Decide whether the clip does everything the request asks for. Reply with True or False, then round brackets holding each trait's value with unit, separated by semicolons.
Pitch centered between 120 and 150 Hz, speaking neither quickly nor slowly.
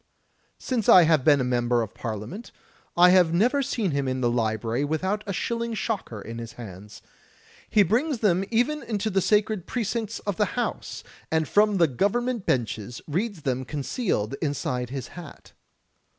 False (175 Hz; 165 wpm)